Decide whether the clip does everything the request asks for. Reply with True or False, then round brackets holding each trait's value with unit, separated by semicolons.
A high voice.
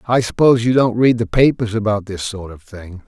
False (110 Hz)